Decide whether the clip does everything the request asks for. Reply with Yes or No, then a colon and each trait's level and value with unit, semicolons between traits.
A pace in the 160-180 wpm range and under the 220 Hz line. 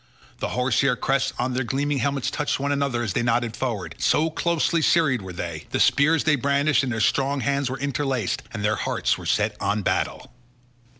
No: average, 200 wpm; low, 135 Hz